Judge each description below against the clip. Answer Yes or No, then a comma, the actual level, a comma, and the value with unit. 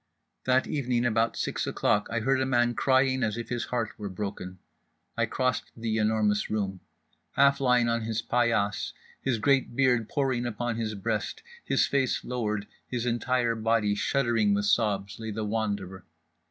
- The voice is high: No, low, 115 Hz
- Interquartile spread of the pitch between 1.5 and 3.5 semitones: Yes, average, 2.8 semitones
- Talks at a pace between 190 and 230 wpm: No, average, 165 wpm